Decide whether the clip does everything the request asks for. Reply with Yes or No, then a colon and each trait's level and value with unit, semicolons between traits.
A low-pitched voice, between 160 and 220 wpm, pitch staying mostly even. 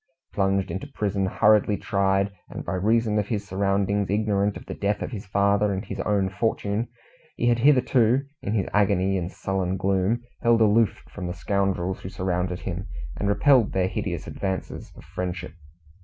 Yes: low, 100 Hz; average, 170 wpm; narrow, 1.9 semitones